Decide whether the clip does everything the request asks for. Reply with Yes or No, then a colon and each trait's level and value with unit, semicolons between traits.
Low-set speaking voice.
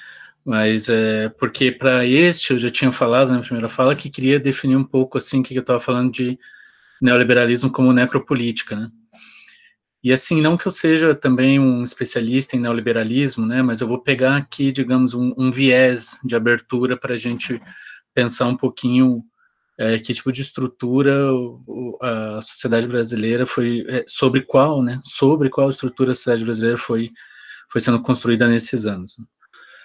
Yes: low, 125 Hz